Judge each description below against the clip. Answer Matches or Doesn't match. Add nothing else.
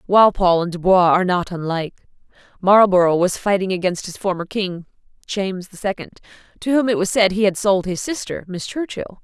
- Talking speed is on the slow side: Doesn't match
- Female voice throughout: Matches